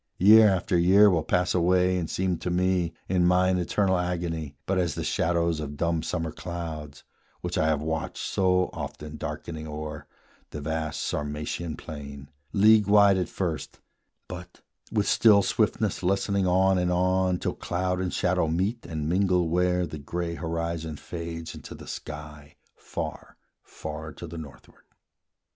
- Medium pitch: No, very low, 85 Hz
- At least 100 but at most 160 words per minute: Yes, average, 155 wpm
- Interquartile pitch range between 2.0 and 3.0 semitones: Yes, average, 2.7 semitones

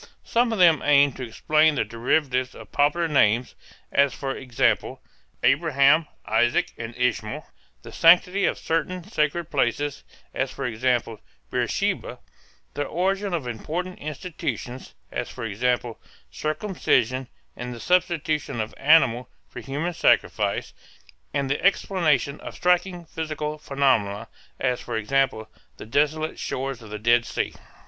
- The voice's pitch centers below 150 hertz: Yes, medium, 140 Hz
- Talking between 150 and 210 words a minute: No, slow, 135 wpm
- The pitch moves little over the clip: No, average, 4.8 semitones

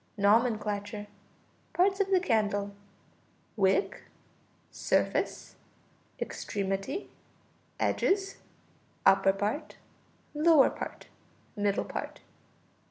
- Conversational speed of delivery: No, slow, 70 wpm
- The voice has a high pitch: Yes, high, 210 Hz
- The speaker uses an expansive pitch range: Yes, wide, 8.5 semitones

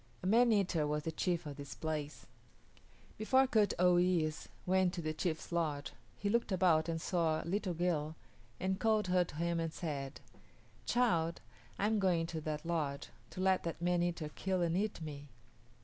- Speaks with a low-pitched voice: No, medium, 170 Hz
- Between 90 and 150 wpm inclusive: No, average, 185 wpm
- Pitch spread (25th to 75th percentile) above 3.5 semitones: No, average, 3.2 semitones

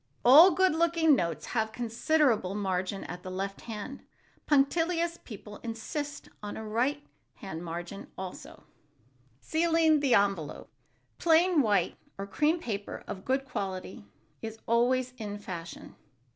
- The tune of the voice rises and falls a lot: Yes, wide, 7.2 semitones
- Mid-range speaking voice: No, high, 230 Hz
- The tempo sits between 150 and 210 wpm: No, slow, 135 wpm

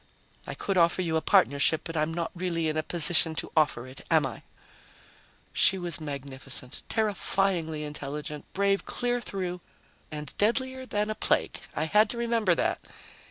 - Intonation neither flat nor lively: Yes, average, 4.6 semitones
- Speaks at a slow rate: No, average, 160 wpm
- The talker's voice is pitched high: No, medium, 170 Hz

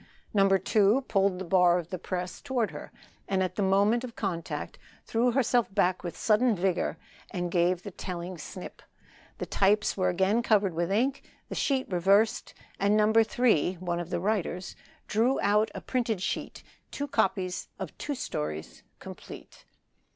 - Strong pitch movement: No, average, 3.5 semitones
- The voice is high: Yes, high, 195 Hz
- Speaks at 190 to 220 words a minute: No, average, 165 wpm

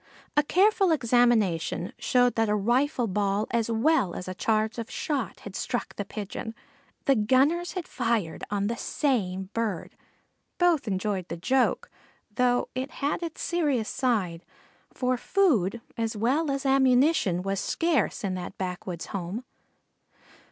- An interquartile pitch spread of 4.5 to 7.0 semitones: Yes, wide, 5.5 semitones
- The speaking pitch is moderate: No, high, 230 Hz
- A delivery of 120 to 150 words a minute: Yes, average, 145 wpm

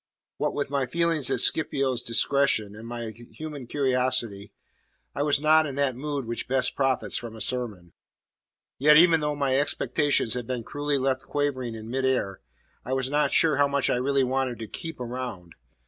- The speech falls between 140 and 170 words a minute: No, average, 180 wpm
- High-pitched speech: No, low, 130 Hz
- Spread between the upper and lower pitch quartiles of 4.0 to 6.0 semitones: No, average, 3.2 semitones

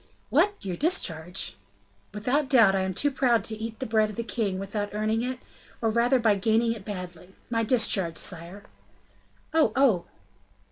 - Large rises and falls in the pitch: No, average, 3.7 semitones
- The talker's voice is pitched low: No, high, 220 Hz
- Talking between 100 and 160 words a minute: No, average, 170 wpm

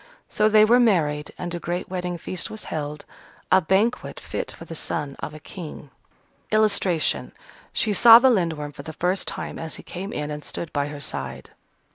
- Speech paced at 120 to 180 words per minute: No, average, 190 wpm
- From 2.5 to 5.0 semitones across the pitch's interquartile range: No, wide, 5.5 semitones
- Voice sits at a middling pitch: Yes, medium, 175 Hz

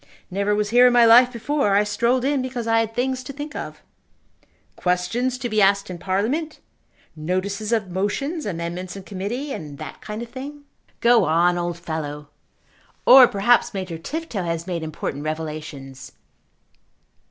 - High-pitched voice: Yes, high, 205 Hz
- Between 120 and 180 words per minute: Yes, average, 160 wpm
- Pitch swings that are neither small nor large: No, wide, 6.0 semitones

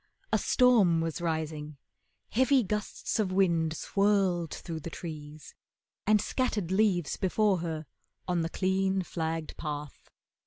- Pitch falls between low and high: Yes, medium, 175 Hz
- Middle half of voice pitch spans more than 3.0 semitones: Yes, average, 3.8 semitones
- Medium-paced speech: No, slow, 125 wpm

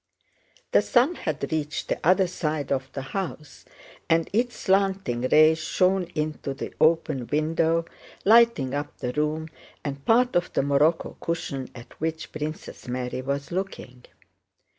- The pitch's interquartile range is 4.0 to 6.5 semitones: Yes, average, 4.6 semitones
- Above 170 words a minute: No, average, 140 wpm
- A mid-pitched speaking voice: Yes, medium, 155 Hz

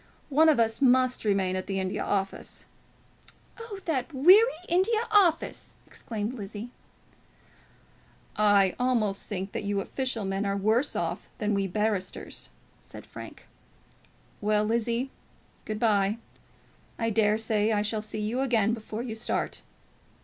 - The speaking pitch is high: Yes, high, 220 Hz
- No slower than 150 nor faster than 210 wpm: No, slow, 135 wpm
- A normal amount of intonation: Yes, average, 3.9 semitones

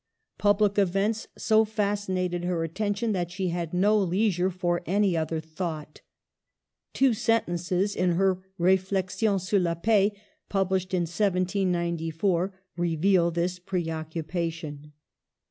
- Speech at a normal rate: No, slow, 115 wpm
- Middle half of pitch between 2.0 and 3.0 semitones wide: Yes, average, 2.7 semitones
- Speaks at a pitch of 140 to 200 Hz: Yes, medium, 185 Hz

